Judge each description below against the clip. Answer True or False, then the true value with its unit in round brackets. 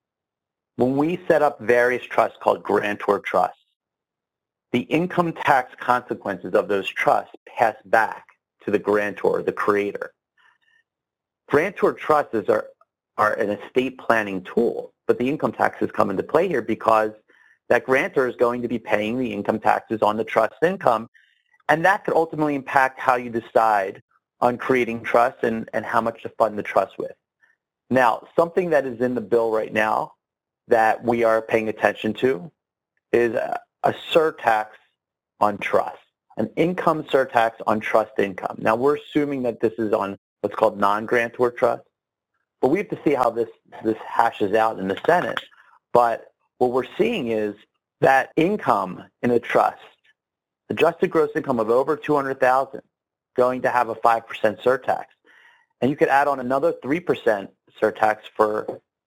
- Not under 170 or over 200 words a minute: False (155 wpm)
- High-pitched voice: False (125 Hz)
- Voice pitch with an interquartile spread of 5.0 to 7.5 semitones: True (5.5 semitones)